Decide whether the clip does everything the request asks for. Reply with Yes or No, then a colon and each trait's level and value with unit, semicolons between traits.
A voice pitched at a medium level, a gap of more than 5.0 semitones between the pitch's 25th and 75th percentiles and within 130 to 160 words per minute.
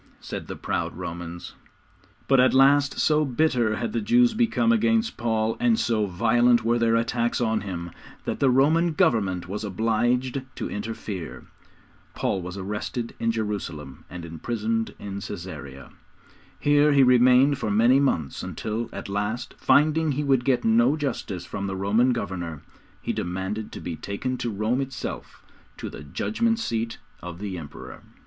No: low, 115 Hz; wide, 5.5 semitones; average, 155 wpm